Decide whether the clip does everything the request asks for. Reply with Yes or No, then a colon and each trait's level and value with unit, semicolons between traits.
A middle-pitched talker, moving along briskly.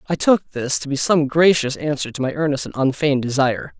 Yes: medium, 145 Hz; fast, 220 wpm